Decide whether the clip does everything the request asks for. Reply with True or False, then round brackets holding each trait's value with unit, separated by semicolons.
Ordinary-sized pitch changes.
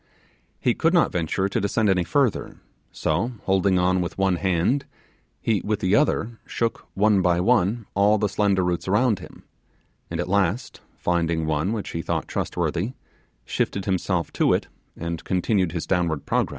True (3.4 semitones)